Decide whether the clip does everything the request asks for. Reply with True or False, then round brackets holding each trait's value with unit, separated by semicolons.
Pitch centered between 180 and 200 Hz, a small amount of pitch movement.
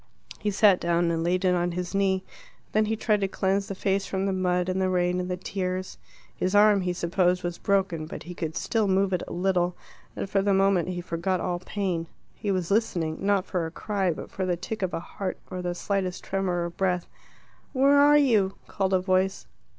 True (185 Hz; 1.8 semitones)